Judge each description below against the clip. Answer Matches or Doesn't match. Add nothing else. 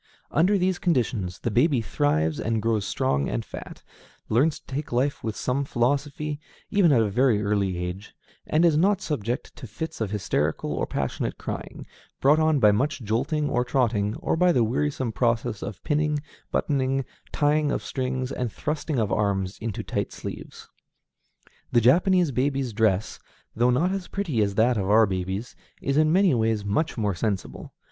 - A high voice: Doesn't match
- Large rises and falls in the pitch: Matches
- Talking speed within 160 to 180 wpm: Matches